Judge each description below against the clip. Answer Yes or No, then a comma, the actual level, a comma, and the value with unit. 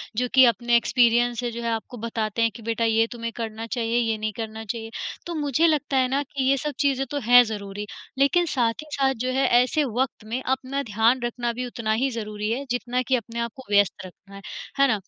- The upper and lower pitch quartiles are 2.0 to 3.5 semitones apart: Yes, average, 2.8 semitones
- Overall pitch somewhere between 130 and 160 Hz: No, high, 235 Hz